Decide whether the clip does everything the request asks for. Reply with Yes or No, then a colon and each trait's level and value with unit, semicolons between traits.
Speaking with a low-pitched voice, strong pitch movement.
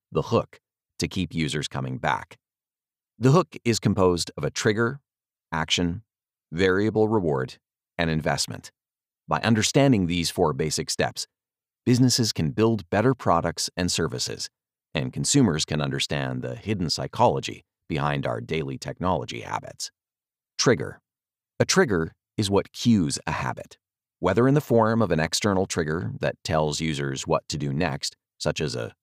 Yes: very low, 90 Hz; wide, 6.2 semitones